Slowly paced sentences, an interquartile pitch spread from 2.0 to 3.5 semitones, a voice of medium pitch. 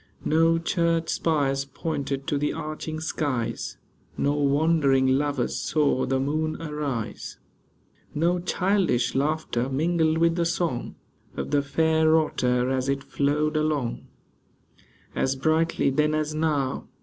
Yes: slow, 125 wpm; average, 2.8 semitones; medium, 150 Hz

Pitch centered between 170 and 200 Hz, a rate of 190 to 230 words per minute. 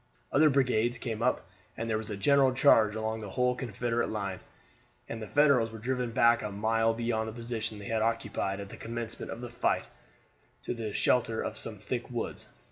No: low, 115 Hz; average, 200 wpm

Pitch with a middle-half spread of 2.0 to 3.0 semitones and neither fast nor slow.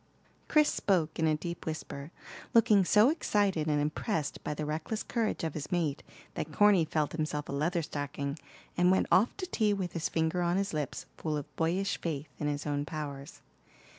No: average, 4.2 semitones; average, 185 wpm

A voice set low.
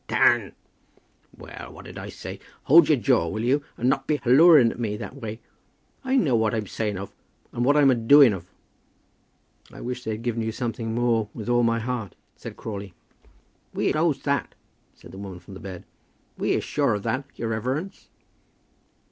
Yes: low, 120 Hz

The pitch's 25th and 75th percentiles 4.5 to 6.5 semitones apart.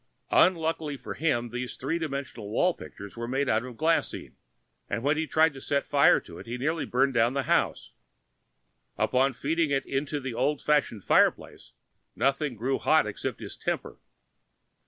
No: average, 3.9 semitones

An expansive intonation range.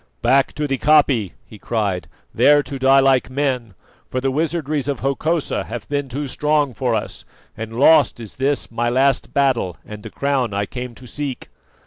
No: average, 3.2 semitones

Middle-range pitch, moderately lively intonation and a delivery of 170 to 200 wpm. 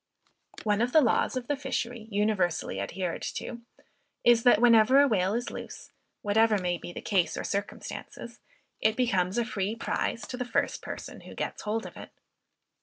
No: high, 220 Hz; average, 3.5 semitones; average, 180 wpm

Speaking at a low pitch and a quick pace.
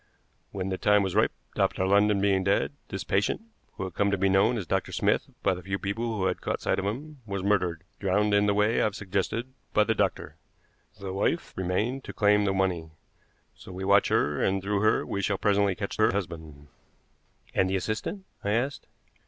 Yes: low, 100 Hz; fast, 210 wpm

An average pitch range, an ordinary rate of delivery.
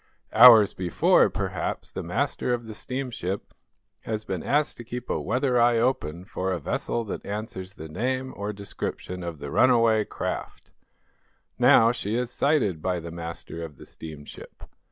No: wide, 5.8 semitones; average, 160 wpm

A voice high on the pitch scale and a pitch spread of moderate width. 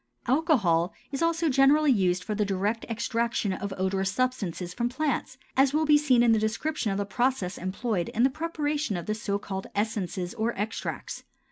No: high, 225 Hz; wide, 5.8 semitones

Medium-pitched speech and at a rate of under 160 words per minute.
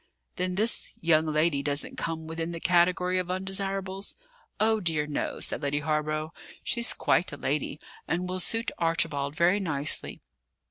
Yes: medium, 165 Hz; average, 150 wpm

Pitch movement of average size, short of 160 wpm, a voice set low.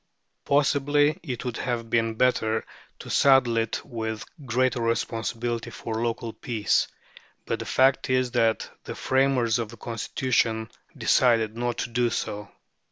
No: narrow, 2.2 semitones; average, 140 wpm; low, 120 Hz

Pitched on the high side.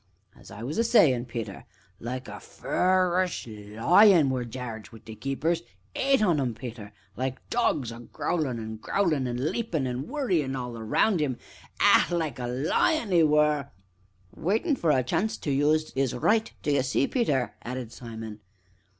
No: low, 135 Hz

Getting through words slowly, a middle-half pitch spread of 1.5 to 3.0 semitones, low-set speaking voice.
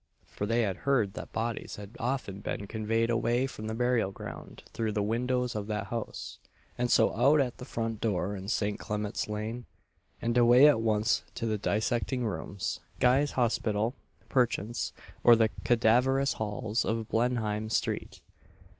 No: average, 160 wpm; narrow, 2.6 semitones; low, 115 Hz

